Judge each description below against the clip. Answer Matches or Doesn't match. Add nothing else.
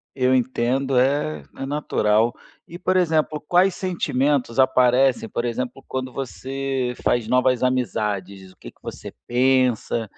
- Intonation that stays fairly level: Matches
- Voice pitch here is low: Matches